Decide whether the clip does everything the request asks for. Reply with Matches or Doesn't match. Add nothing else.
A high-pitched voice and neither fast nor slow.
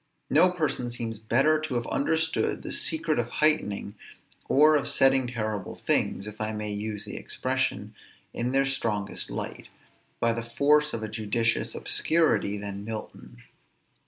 Doesn't match